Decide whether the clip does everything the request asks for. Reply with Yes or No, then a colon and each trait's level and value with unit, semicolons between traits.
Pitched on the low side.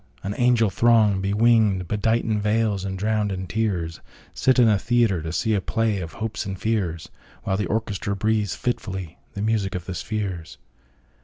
Yes: low, 105 Hz